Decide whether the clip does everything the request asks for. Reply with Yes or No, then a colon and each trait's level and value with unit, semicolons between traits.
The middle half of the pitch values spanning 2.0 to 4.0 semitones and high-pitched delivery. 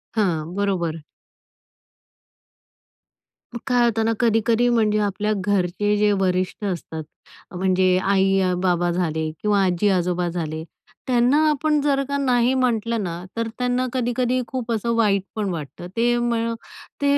No: average, 4.9 semitones; high, 210 Hz